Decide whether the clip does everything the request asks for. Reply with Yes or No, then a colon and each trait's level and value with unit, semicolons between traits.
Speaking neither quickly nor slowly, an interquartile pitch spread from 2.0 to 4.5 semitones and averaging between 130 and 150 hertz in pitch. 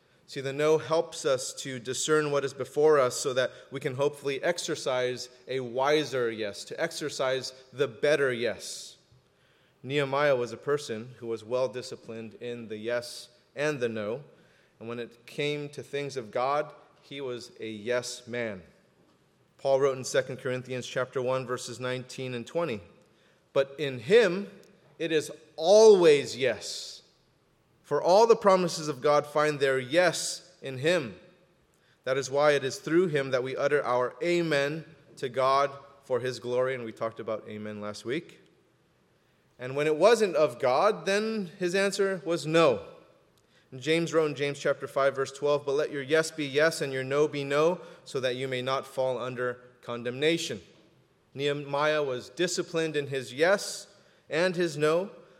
Yes: average, 165 wpm; average, 4.0 semitones; medium, 140 Hz